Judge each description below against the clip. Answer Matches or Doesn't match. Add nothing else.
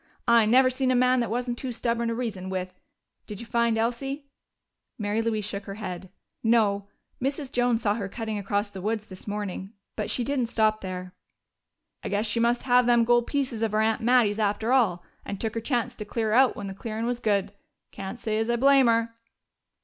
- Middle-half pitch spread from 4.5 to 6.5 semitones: Doesn't match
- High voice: Matches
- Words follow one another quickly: Matches